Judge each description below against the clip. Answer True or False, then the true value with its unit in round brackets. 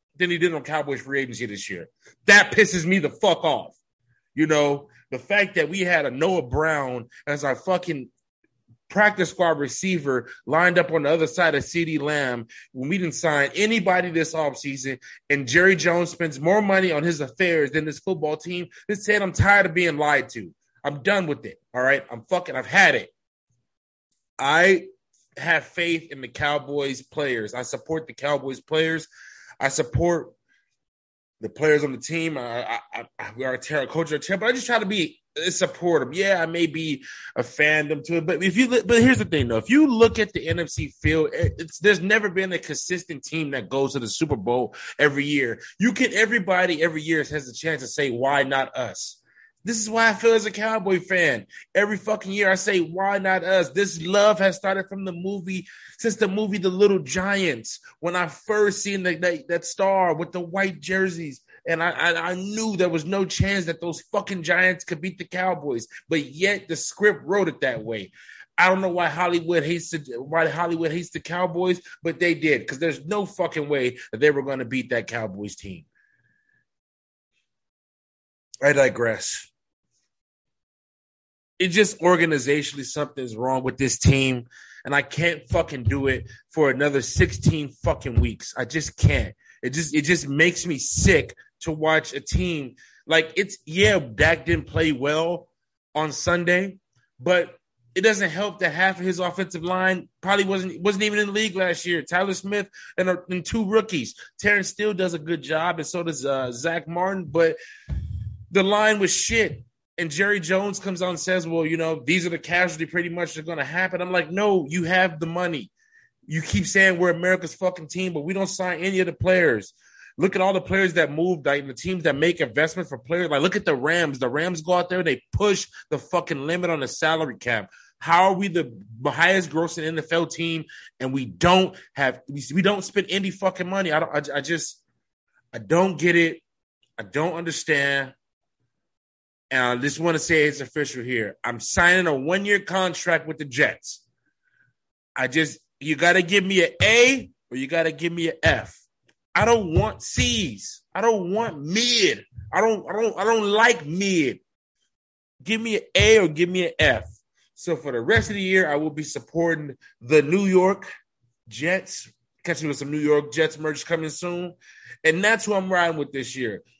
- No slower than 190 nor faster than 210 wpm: True (195 wpm)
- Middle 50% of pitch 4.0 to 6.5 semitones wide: True (4.4 semitones)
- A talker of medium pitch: True (170 Hz)